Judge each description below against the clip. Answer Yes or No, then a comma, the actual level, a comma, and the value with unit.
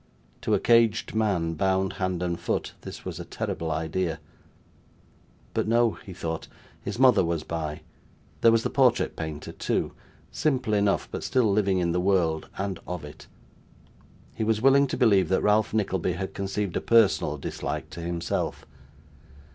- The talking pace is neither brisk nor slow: Yes, average, 165 wpm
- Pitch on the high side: No, very low, 95 Hz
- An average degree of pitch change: Yes, average, 4.6 semitones